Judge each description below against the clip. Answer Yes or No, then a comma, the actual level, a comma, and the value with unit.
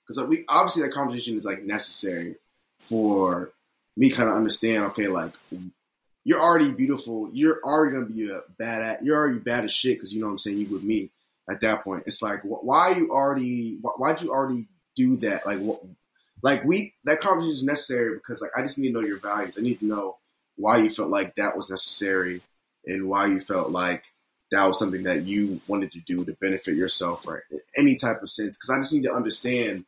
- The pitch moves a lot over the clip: Yes, wide, 6.0 semitones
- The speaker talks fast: Yes, fast, 220 wpm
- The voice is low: Yes, low, 115 Hz